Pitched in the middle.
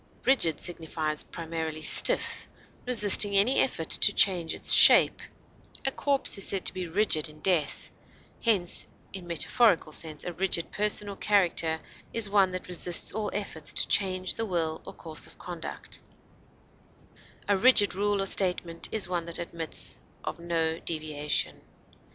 Yes: medium, 180 Hz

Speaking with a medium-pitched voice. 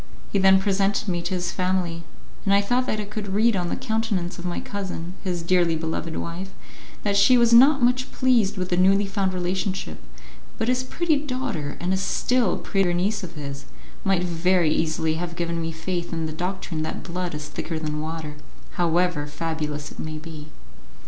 Yes: medium, 180 Hz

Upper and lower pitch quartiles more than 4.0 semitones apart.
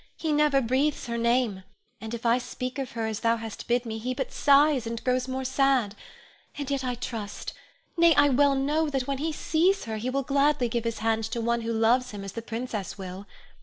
No: average, 3.4 semitones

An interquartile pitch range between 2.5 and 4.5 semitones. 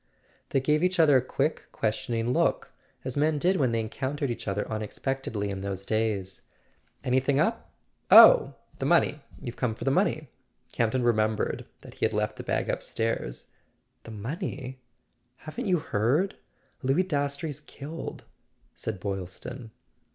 No: average, 5.0 semitones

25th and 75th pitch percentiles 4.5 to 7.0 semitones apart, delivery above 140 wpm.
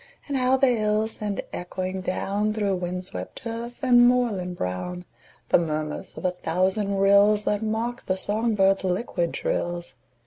No: average, 3.7 semitones; average, 160 wpm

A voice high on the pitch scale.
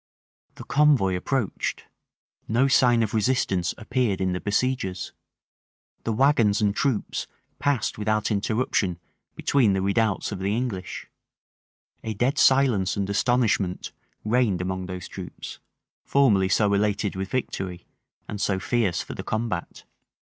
No: low, 105 Hz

